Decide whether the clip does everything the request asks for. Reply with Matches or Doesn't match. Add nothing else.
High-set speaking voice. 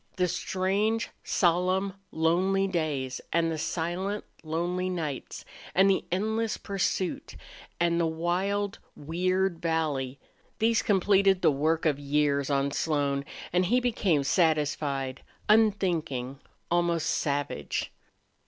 Doesn't match